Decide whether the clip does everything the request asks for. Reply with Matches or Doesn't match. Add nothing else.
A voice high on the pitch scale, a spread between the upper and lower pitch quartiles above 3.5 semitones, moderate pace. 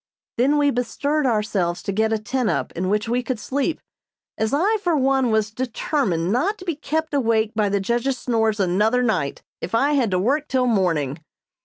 Matches